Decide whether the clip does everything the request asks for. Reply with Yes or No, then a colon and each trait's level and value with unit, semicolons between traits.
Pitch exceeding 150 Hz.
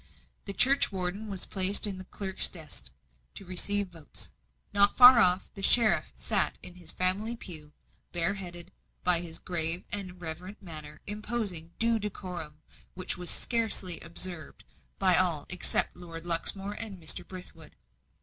Yes: medium, 185 Hz